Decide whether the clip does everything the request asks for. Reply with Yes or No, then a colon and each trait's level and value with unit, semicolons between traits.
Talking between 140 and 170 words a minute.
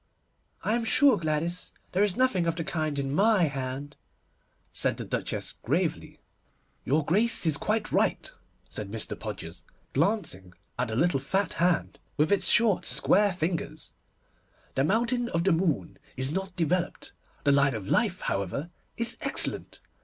Yes: average, 155 wpm